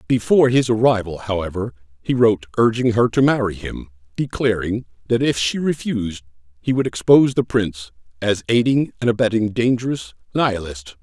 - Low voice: Yes, low, 110 Hz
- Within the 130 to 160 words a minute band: Yes, average, 145 wpm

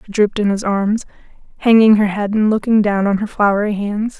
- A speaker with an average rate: No, fast, 215 wpm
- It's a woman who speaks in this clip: Yes, female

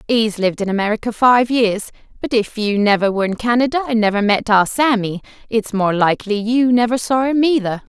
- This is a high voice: Yes, high, 225 Hz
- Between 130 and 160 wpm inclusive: No, average, 195 wpm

